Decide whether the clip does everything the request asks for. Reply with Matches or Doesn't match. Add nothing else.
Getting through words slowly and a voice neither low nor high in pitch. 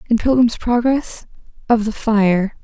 Doesn't match